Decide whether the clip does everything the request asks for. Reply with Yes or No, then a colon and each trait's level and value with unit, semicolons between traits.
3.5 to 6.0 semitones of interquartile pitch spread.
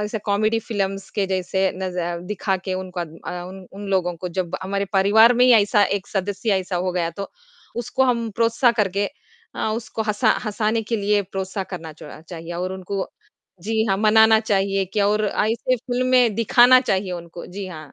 No: average, 2.9 semitones